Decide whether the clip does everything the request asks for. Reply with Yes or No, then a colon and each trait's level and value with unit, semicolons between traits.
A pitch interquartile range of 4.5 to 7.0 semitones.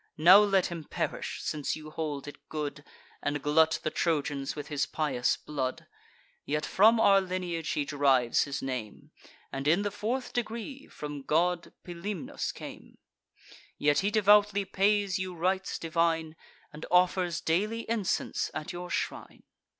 Yes: average, 4.8 semitones